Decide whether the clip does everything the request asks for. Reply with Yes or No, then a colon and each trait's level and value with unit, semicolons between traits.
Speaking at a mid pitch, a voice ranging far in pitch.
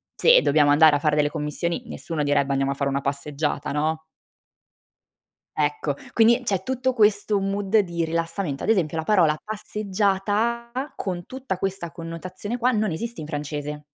Yes: medium, 170 Hz; wide, 6.1 semitones